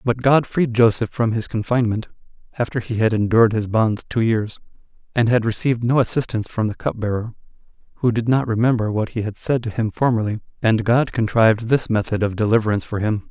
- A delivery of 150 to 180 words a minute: No, average, 195 wpm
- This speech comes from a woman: No, male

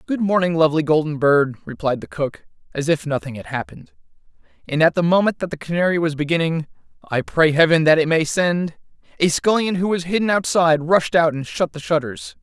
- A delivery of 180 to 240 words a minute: Yes, average, 200 wpm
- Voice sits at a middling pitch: Yes, medium, 160 Hz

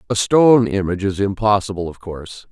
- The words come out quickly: No, average, 165 wpm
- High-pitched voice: No, low, 100 Hz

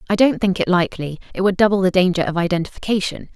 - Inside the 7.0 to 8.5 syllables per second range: Yes, 7.1 syllables/s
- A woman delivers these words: Yes, female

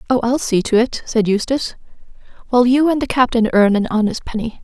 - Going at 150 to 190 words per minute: No, fast, 205 wpm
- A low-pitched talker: No, high, 235 Hz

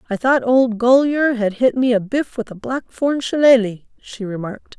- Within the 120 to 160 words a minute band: No, average, 190 wpm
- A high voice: Yes, high, 240 Hz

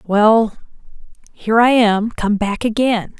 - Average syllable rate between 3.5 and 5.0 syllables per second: Yes, 4.0 syllables/s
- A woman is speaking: Yes, female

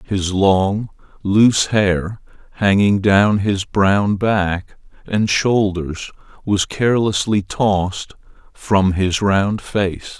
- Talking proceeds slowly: Yes, slow, 105 wpm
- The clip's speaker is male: Yes, male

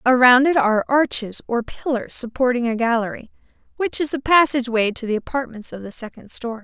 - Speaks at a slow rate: No, average, 190 wpm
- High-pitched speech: Yes, high, 245 Hz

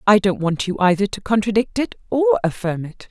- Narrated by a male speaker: No, female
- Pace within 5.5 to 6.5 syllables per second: Yes, 5.6 syllables/s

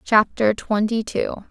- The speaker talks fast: No, slow, 120 wpm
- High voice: Yes, high, 220 Hz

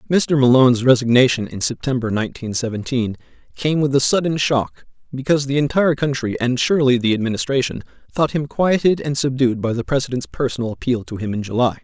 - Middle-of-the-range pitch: No, low, 130 Hz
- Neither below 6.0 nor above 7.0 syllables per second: Yes, 6.1 syllables/s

